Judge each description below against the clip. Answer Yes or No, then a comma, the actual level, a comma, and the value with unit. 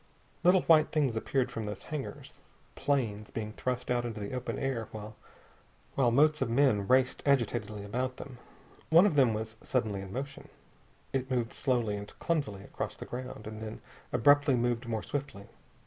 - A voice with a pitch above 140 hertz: No, low, 120 Hz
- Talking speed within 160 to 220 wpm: Yes, average, 165 wpm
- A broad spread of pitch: No, average, 4.0 semitones